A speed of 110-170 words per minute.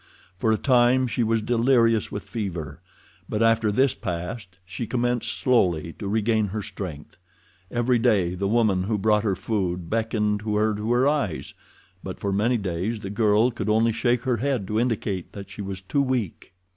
No: average, 180 wpm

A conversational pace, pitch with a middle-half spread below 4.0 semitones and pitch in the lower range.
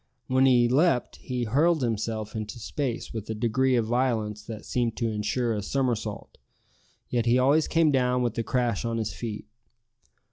Yes: average, 175 wpm; average, 2.7 semitones; low, 120 Hz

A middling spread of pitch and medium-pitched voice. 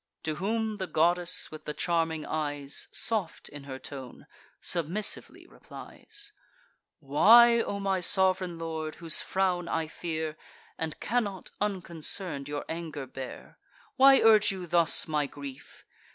Yes: average, 4.3 semitones; medium, 170 Hz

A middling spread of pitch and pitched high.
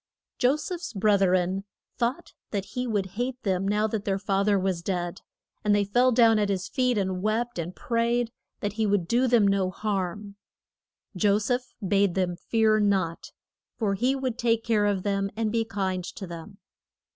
Yes: average, 3.2 semitones; high, 205 Hz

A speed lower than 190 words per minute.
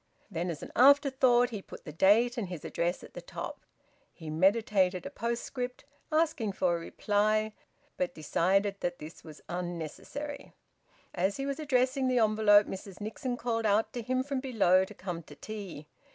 Yes: average, 170 wpm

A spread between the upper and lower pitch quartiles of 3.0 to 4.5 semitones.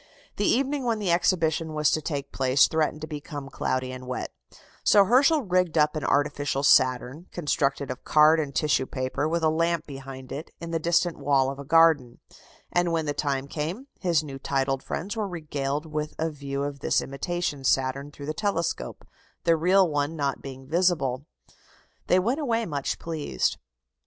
Yes: average, 3.6 semitones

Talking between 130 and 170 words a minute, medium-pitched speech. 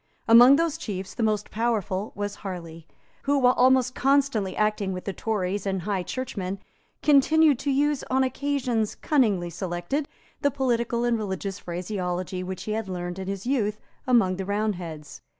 No: average, 160 wpm; high, 210 Hz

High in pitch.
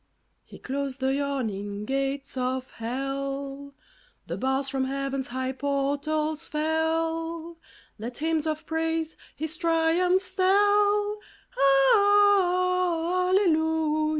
Yes: very high, 310 Hz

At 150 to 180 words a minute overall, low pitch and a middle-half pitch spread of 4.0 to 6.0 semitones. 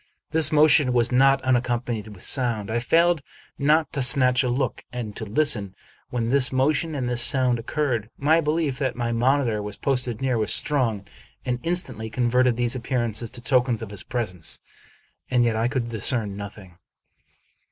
No: average, 175 wpm; low, 125 Hz; average, 3.1 semitones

